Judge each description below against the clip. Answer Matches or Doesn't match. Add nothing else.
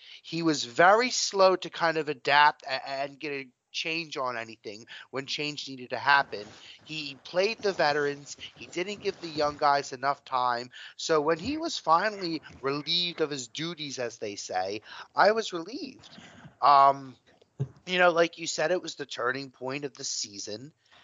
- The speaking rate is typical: Matches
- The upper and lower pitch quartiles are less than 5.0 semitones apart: Matches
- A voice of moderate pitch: Matches